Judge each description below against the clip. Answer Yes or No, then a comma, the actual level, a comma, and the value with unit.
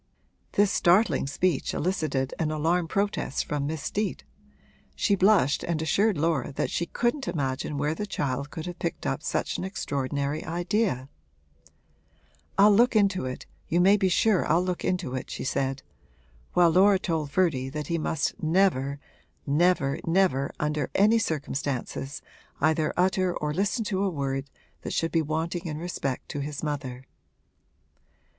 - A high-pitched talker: No, medium, 160 Hz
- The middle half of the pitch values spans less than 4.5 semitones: No, average, 4.8 semitones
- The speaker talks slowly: No, average, 155 wpm